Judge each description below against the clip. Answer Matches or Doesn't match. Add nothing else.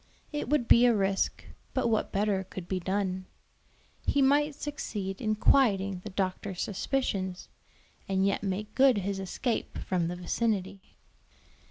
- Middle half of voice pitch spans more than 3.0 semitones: Matches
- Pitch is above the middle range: Matches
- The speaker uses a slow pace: Doesn't match